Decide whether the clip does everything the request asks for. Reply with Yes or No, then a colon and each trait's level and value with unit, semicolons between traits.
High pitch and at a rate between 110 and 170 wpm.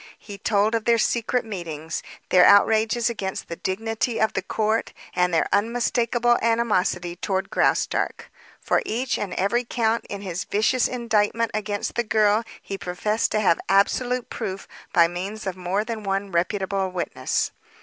Yes: high, 210 Hz; average, 155 wpm